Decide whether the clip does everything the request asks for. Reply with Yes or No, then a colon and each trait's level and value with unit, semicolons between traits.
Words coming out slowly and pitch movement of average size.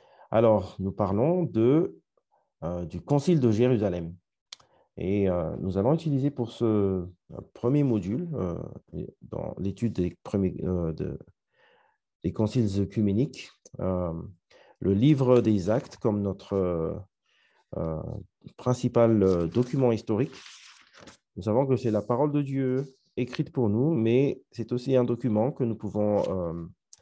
Yes: slow, 135 wpm; average, 4.8 semitones